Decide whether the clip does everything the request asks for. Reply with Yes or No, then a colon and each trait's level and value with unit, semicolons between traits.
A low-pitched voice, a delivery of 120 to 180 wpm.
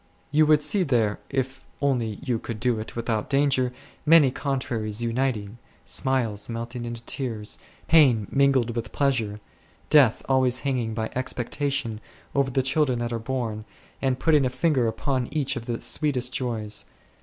Yes: low, 125 Hz; average, 155 wpm